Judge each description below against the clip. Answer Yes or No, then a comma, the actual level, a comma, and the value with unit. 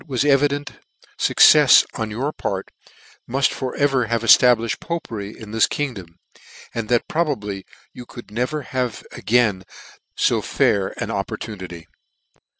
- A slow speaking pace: Yes, slow, 130 wpm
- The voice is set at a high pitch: No, low, 115 Hz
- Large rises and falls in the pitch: No, average, 4.5 semitones